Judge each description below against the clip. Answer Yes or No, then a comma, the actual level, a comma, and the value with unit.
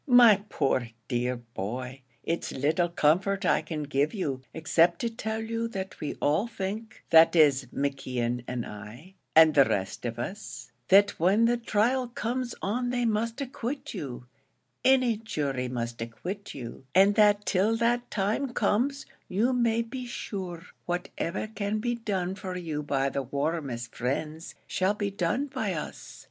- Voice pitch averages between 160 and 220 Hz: Yes, medium, 185 Hz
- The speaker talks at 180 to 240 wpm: No, average, 155 wpm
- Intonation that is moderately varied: No, wide, 8.2 semitones